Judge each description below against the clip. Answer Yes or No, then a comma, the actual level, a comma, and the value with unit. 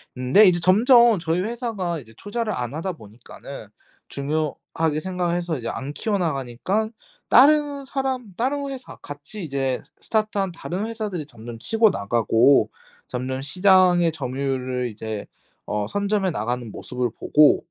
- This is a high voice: No, medium, 170 Hz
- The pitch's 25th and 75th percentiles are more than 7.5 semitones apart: Yes, wide, 8.7 semitones